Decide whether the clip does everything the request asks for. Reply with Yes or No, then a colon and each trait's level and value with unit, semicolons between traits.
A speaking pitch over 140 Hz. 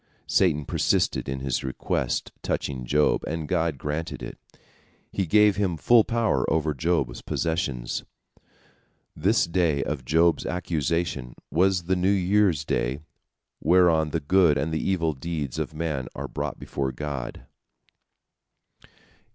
No: very low, 80 Hz